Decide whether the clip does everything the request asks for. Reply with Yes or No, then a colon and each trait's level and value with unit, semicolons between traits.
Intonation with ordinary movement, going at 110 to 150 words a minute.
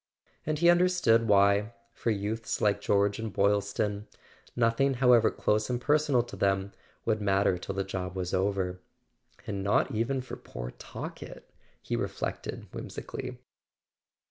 Yes: average, 3.4 semitones; average, 140 wpm